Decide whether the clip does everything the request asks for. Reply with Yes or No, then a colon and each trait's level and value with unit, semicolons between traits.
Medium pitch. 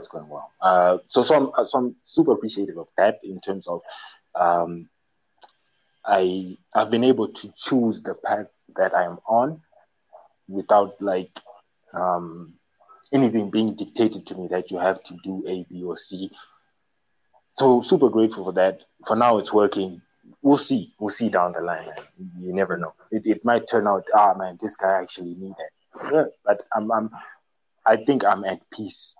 No: very low, 95 Hz